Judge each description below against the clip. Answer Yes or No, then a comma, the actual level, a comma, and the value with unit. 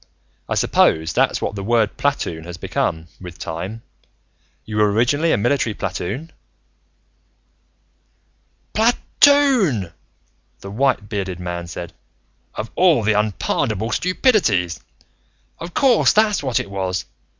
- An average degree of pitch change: No, wide, 8.1 semitones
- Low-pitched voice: Yes, low, 110 Hz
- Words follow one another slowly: Yes, slow, 120 wpm